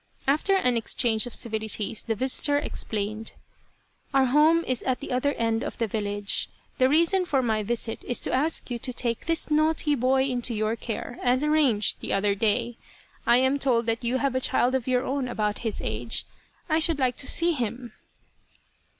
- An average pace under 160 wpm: No, average, 195 wpm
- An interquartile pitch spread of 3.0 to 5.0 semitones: Yes, average, 3.8 semitones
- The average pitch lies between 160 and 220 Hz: No, very high, 250 Hz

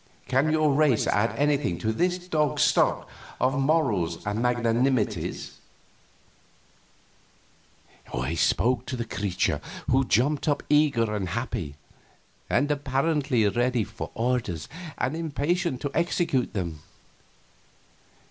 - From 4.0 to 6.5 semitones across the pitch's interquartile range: Yes, average, 5.1 semitones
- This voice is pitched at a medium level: No, low, 125 Hz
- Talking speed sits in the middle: No, slow, 110 wpm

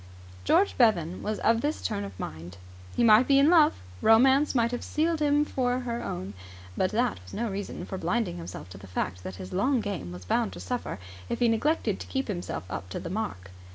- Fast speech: Yes, fast, 220 wpm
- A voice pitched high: Yes, high, 220 Hz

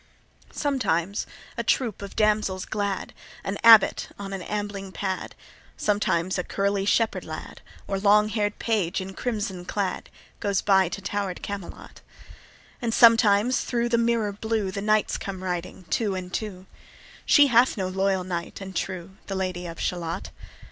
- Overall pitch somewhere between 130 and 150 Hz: No, high, 200 Hz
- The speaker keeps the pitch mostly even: Yes, narrow, 2.3 semitones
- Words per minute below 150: No, average, 155 wpm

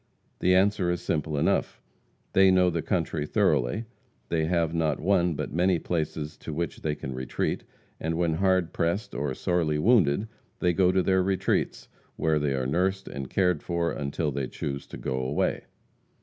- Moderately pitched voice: No, very low, 85 Hz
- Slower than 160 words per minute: No, average, 175 wpm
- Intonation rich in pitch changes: No, average, 3.7 semitones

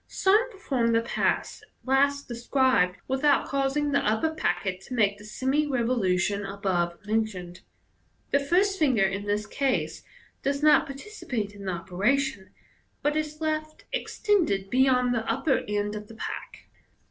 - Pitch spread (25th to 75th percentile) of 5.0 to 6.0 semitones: Yes, wide, 5.6 semitones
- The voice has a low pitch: No, very high, 250 Hz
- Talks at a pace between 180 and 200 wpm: No, average, 145 wpm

